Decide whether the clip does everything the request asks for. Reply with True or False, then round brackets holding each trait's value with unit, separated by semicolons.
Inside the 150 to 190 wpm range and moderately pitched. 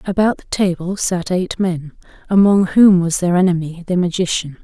True (170 wpm; 180 Hz)